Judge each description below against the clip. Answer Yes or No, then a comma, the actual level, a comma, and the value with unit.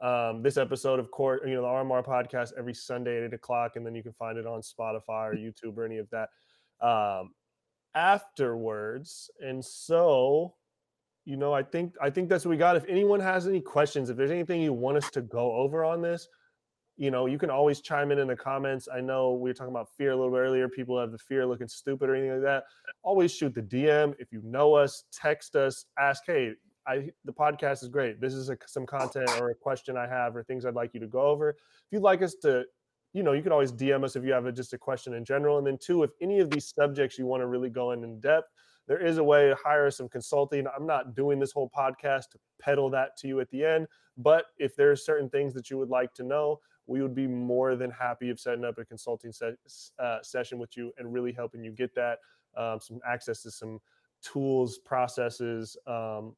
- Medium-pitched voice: No, low, 130 Hz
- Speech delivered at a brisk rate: Yes, fast, 240 wpm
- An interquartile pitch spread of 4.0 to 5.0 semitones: No, average, 3.2 semitones